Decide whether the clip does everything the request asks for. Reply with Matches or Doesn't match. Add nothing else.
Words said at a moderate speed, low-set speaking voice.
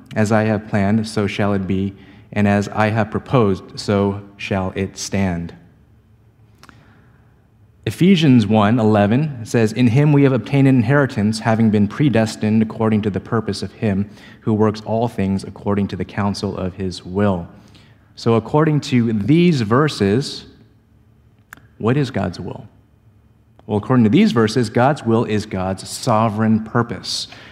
Matches